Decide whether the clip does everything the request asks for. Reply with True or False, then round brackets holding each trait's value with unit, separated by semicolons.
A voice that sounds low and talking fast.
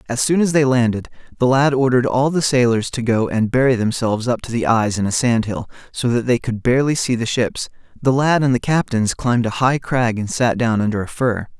True (120 Hz; 240 wpm)